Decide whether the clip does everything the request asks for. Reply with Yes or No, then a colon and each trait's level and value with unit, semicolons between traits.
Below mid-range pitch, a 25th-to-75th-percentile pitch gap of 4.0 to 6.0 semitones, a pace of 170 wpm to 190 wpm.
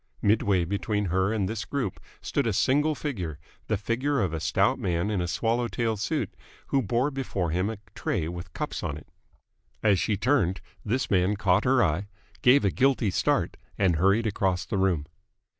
Yes: low, 100 Hz; average, 4.6 semitones; average, 185 wpm